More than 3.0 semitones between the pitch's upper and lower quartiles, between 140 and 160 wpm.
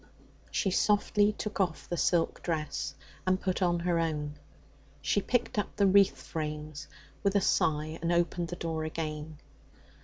Yes: average, 3.6 semitones; average, 155 wpm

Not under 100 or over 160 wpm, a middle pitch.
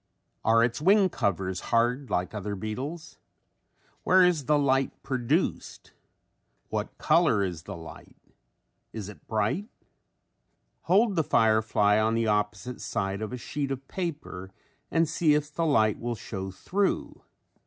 No: average, 140 wpm; low, 120 Hz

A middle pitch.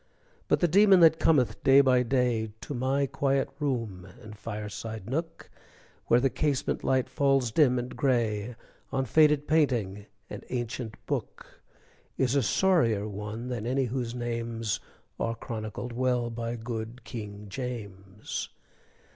No: low, 120 Hz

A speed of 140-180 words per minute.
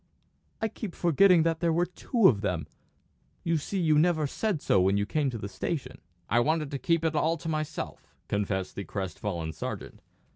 No: average, 190 wpm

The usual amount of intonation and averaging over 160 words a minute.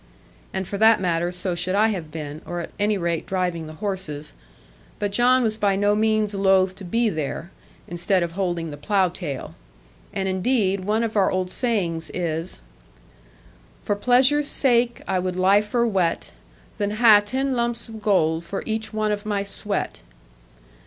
Yes: average, 3.7 semitones; average, 170 wpm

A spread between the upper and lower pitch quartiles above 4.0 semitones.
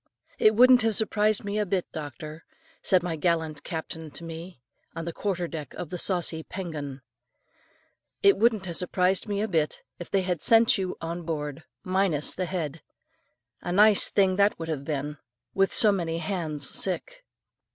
No: average, 3.7 semitones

